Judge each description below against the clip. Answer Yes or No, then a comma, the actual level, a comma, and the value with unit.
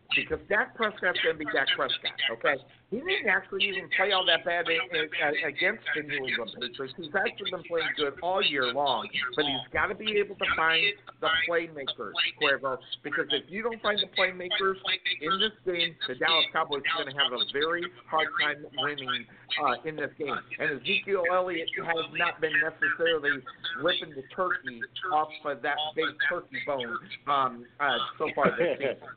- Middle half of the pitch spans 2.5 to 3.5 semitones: No, average, 4.1 semitones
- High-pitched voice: No, medium, 175 Hz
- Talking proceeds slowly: No, average, 185 wpm